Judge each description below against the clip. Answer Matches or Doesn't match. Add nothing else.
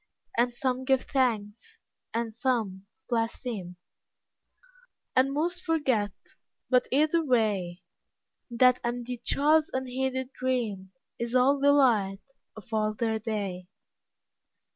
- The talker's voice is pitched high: Matches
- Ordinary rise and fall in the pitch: Matches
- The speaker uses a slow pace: Matches